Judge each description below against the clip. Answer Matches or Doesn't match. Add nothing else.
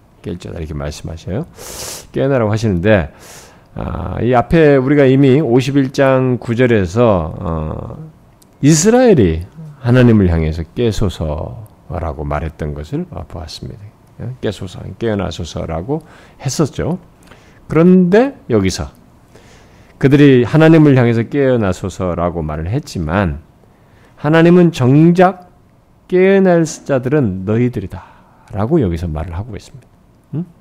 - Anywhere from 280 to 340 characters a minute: Doesn't match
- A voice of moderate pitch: Doesn't match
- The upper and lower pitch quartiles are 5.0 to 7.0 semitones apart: Doesn't match